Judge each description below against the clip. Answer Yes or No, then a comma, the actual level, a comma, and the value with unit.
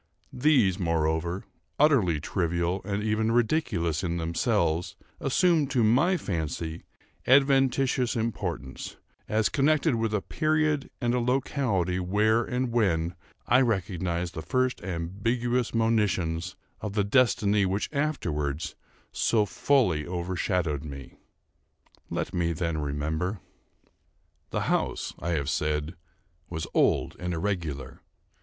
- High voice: No, very low, 95 Hz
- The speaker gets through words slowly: Yes, slow, 115 wpm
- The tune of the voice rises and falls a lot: Yes, wide, 6.5 semitones